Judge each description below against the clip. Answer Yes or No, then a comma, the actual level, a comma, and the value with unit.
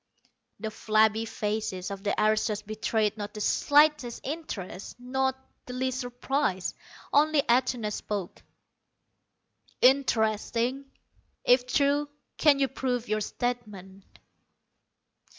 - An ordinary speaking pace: No, slow, 100 wpm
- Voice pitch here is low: No, high, 235 Hz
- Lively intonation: No, average, 3.9 semitones